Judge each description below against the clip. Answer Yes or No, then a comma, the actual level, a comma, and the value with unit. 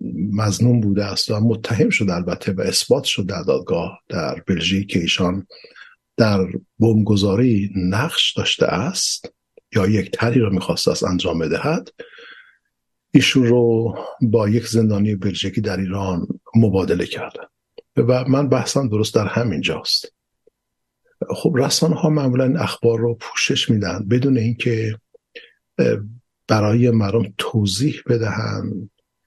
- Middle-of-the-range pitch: No, low, 115 Hz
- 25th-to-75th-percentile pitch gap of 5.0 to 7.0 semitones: No, average, 4.2 semitones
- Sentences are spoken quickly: No, average, 125 wpm